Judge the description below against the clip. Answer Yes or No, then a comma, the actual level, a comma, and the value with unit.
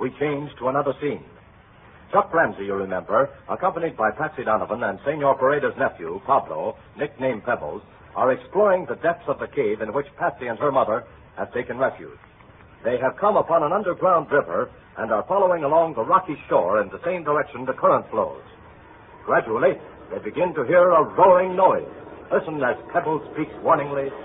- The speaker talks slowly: No, average, 175 wpm